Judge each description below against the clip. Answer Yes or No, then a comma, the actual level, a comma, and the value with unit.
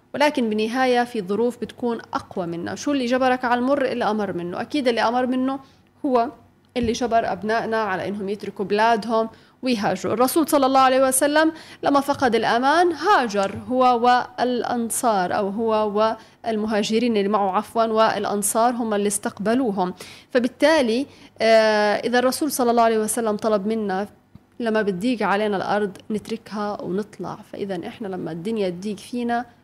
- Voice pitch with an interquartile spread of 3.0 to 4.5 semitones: Yes, average, 3.3 semitones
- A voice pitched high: Yes, high, 225 Hz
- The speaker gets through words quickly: Yes, fast, 140 wpm